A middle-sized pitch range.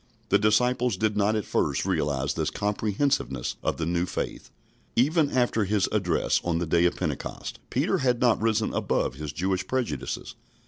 No: wide, 6.2 semitones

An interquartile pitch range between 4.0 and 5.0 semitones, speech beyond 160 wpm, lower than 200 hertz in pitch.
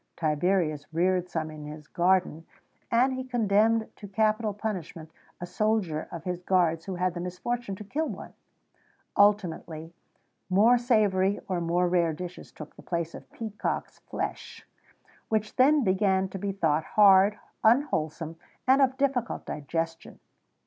No: average, 4.5 semitones; average, 145 wpm; high, 190 Hz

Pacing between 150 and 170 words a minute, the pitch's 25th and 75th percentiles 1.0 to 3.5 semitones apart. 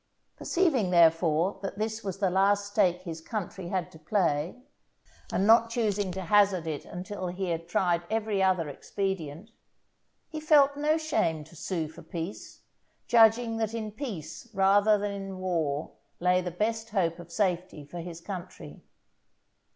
No: average, 155 wpm; average, 4.0 semitones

